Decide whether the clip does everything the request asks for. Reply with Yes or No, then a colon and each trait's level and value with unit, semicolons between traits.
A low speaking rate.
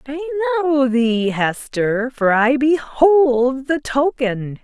Yes: slow, 115 wpm